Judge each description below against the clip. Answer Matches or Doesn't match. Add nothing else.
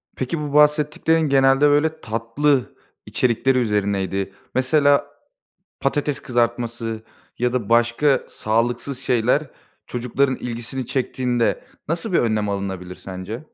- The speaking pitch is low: Matches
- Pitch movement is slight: Doesn't match